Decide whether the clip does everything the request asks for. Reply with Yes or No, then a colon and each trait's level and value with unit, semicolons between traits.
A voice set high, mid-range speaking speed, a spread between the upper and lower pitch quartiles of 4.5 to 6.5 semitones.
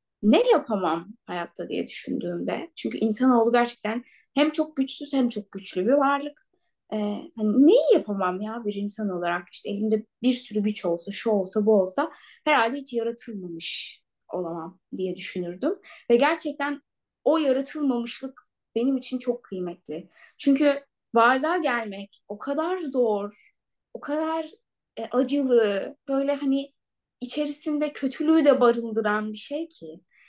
Yes: high, 240 Hz; average, 130 wpm; wide, 5.5 semitones